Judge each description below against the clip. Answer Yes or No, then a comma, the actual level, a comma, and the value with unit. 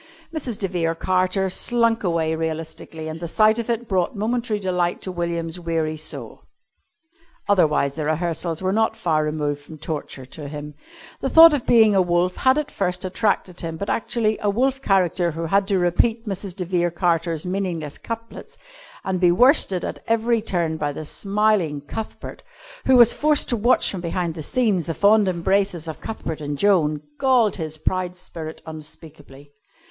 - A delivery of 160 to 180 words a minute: Yes, average, 175 wpm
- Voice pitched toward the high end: No, medium, 180 Hz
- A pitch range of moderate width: Yes, average, 4.9 semitones